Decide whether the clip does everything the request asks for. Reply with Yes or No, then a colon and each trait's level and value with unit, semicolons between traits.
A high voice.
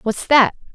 Yes: high, 235 Hz